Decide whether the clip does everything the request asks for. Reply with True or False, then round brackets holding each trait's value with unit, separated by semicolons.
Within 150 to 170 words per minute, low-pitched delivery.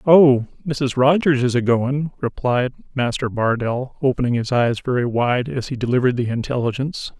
True (160 wpm; 130 Hz)